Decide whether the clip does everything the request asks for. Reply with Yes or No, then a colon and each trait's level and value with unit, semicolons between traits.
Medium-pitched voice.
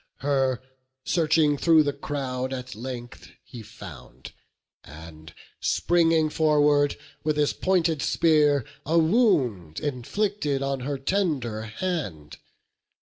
Yes: medium, 145 Hz